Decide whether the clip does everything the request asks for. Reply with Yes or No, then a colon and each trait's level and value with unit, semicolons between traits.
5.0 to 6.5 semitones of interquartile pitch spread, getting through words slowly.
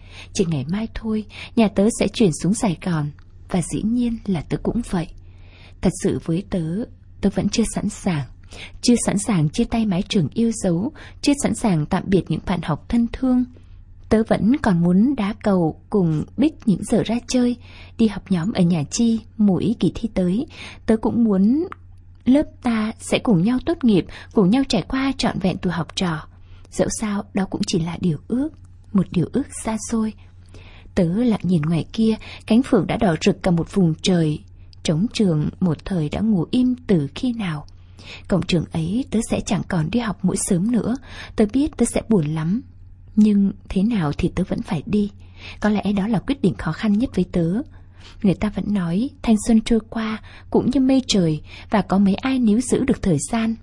No: wide, 5.5 semitones; average, 205 wpm